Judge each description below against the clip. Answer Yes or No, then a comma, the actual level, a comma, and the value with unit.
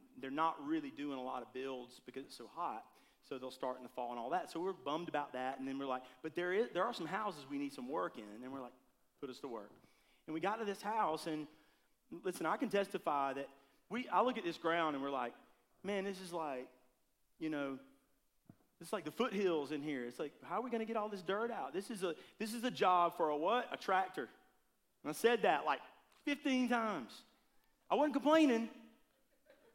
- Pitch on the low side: No, medium, 170 Hz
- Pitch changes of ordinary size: No, wide, 8.4 semitones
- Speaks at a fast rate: Yes, fast, 235 wpm